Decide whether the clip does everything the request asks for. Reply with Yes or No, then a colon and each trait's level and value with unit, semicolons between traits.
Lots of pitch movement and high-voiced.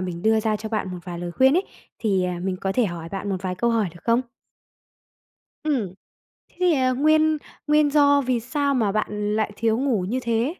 Yes: wide, 5.9 semitones; high, 225 Hz